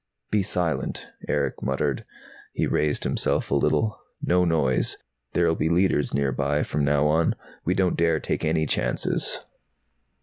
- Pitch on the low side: Yes, very low, 80 Hz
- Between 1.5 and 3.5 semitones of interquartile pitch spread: Yes, average, 3.2 semitones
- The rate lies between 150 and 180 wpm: No, average, 140 wpm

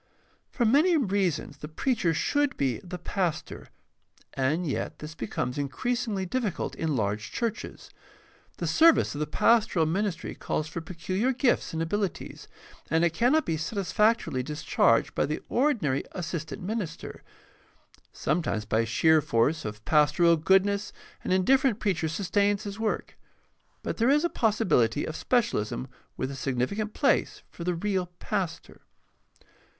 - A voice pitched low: No, medium, 180 Hz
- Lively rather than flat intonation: Yes, wide, 6.1 semitones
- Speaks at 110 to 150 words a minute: Yes, average, 145 wpm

